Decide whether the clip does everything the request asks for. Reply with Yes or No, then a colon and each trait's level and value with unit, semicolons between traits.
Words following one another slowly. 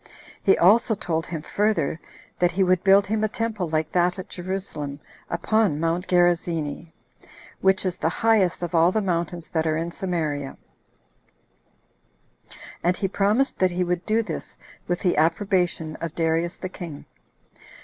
No: average, 155 wpm